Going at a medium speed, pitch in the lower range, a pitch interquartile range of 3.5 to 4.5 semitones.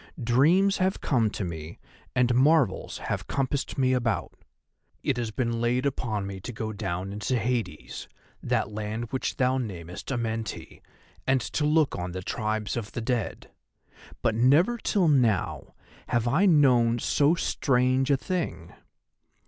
Yes: average, 150 wpm; low, 120 Hz; average, 3.9 semitones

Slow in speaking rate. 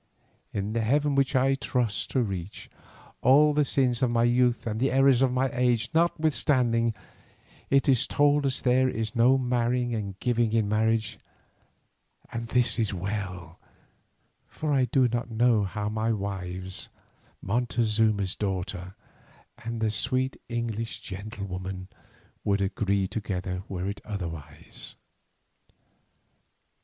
Yes: slow, 130 wpm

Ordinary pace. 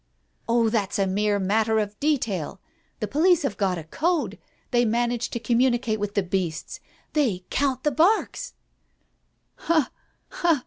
Yes: average, 150 wpm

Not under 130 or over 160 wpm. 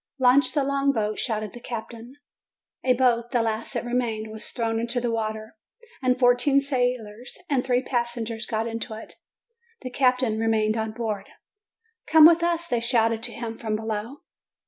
No: average, 170 wpm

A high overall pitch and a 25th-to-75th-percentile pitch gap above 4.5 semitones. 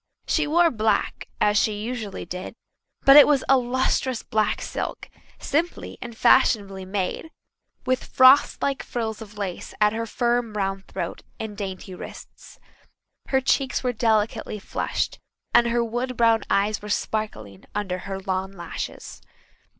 No: high, 220 Hz; average, 3.9 semitones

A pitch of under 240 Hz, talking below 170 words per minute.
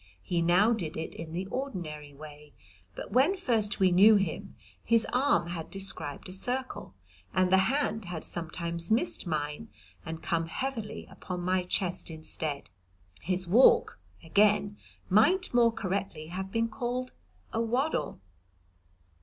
Yes: high, 190 Hz; average, 140 wpm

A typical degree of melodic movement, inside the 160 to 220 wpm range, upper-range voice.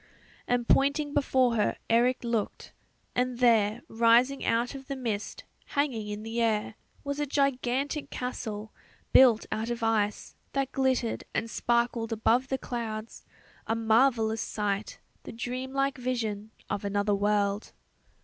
No: average, 3.0 semitones; average, 140 wpm; high, 235 Hz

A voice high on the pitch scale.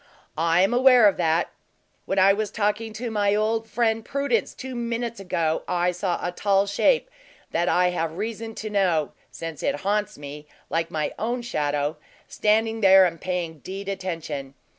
Yes: high, 195 Hz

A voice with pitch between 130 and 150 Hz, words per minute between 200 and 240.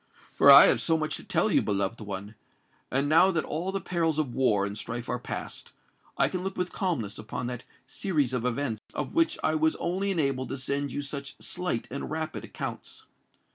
Yes: medium, 140 Hz; fast, 205 wpm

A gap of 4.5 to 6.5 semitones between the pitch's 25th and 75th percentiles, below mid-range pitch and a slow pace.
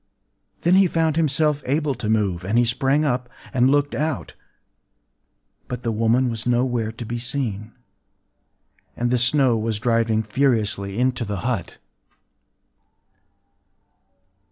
No: average, 3.6 semitones; low, 120 Hz; slow, 130 wpm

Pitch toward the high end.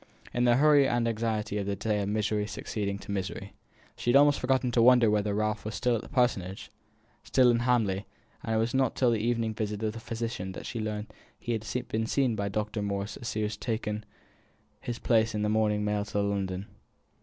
No: low, 110 Hz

